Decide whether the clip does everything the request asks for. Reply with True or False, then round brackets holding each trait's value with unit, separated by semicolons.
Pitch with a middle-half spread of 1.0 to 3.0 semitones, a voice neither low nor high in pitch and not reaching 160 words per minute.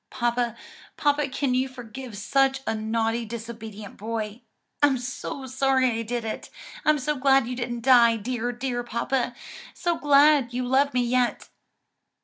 False (2.5 semitones; 245 Hz; 150 wpm)